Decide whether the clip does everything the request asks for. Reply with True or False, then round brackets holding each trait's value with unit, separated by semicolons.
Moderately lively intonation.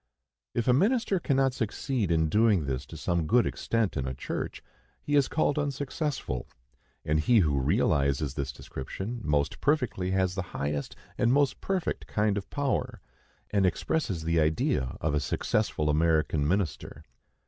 False (9.0 semitones)